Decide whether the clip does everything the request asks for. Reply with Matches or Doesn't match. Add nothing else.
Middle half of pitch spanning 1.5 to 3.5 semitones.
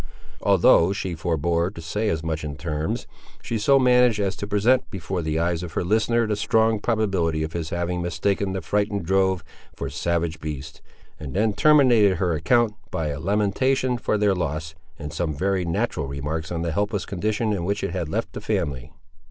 Doesn't match